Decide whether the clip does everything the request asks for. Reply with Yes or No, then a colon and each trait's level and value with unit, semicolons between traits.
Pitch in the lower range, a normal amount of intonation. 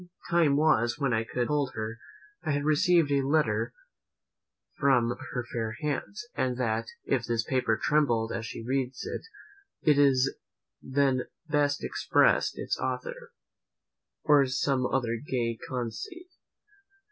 Yes: low, 130 Hz; average, 3.7 semitones